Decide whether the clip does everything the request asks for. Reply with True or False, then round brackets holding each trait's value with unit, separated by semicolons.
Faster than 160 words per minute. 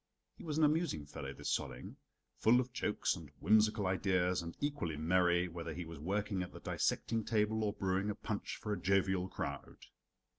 True (185 wpm)